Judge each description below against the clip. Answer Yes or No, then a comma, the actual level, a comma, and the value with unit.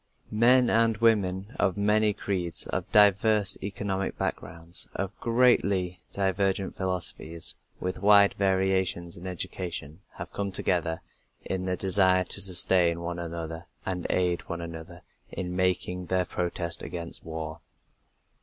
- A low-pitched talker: Yes, very low, 95 Hz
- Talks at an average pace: No, slow, 125 wpm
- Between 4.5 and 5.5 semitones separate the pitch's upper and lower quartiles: No, narrow, 2.5 semitones